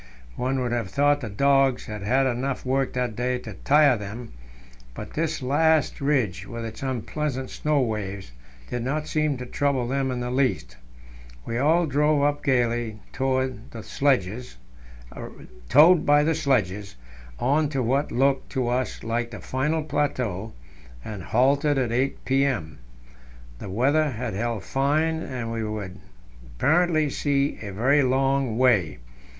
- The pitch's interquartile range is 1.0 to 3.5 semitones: No, average, 3.9 semitones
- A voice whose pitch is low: Yes, low, 130 Hz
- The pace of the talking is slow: No, average, 145 wpm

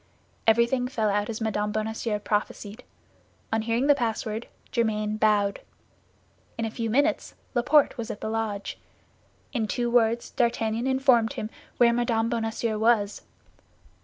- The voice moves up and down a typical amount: No, narrow, 1.8 semitones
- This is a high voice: Yes, high, 225 Hz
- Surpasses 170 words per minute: No, slow, 135 wpm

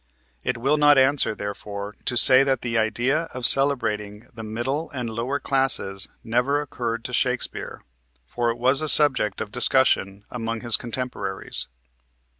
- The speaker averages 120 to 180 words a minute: Yes, average, 150 wpm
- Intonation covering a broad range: No, average, 3.4 semitones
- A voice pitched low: Yes, low, 120 Hz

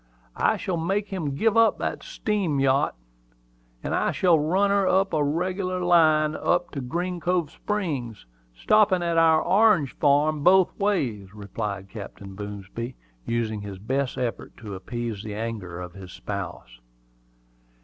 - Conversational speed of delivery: Yes, average, 150 wpm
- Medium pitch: Yes, medium, 145 Hz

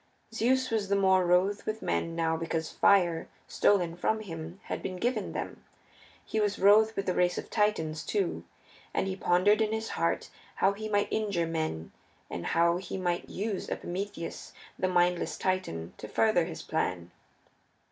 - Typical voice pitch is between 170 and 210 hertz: Yes, medium, 185 Hz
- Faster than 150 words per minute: Yes, average, 165 wpm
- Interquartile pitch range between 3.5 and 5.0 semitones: Yes, average, 3.8 semitones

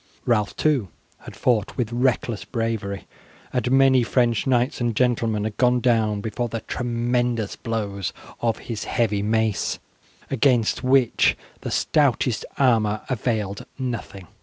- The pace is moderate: No, slow, 130 wpm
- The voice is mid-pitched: No, low, 115 Hz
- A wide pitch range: No, narrow, 2.6 semitones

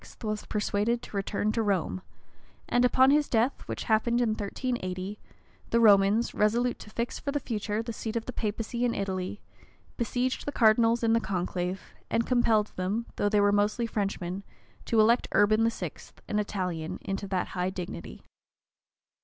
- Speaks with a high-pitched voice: Yes, high, 215 Hz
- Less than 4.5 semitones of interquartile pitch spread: Yes, average, 2.8 semitones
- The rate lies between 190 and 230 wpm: No, average, 165 wpm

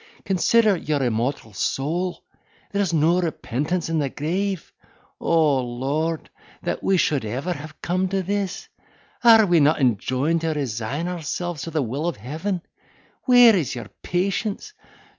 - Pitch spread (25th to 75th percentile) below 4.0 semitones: No, average, 4.7 semitones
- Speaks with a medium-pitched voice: Yes, medium, 165 Hz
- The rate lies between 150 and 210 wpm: No, slow, 135 wpm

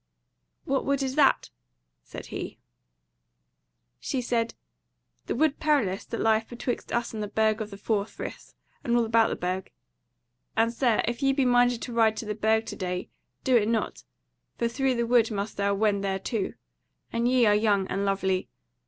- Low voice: No, high, 225 Hz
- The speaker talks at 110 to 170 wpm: No, average, 180 wpm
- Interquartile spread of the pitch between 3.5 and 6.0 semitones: No, average, 2.8 semitones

